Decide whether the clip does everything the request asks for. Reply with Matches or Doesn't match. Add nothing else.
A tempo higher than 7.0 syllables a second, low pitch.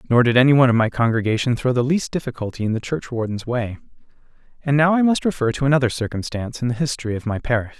Matches